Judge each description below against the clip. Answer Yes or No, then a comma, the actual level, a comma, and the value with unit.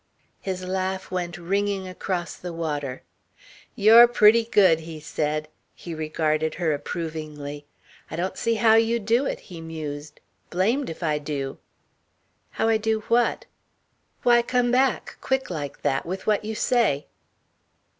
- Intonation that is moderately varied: No, wide, 6.1 semitones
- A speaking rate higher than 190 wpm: No, average, 145 wpm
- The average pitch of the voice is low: No, medium, 180 Hz